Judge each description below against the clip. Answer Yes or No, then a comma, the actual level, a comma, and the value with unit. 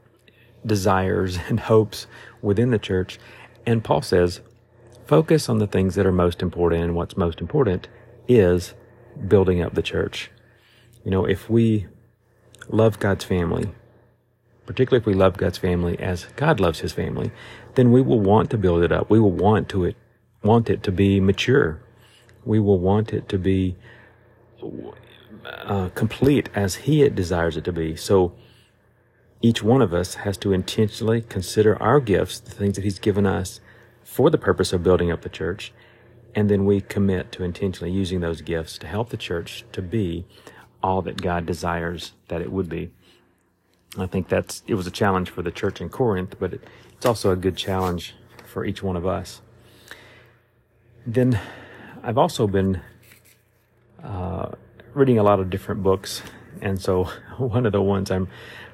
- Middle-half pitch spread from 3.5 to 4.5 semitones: Yes, average, 4.1 semitones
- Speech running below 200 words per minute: Yes, average, 170 wpm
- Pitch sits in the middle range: No, low, 105 Hz